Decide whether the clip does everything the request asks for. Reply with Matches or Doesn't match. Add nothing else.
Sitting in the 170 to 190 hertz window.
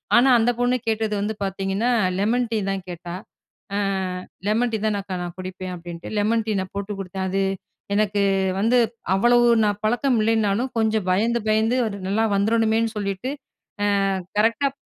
Doesn't match